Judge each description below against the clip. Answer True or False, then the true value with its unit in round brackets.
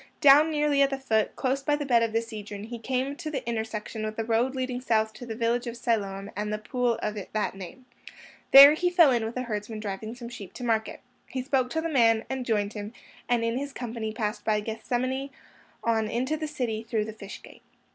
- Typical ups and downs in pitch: True (3.2 semitones)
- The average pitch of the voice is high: True (235 Hz)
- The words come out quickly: True (225 wpm)